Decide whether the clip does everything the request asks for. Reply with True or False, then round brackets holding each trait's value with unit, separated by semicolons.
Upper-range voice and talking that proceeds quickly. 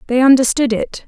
False (255 Hz; 170 wpm)